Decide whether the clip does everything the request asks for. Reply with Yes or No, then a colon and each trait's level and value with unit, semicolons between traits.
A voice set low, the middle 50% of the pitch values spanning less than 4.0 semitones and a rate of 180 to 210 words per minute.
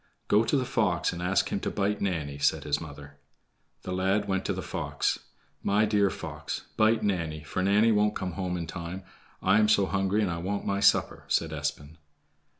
Yes: very low, 95 Hz; average, 3.5 semitones; average, 200 wpm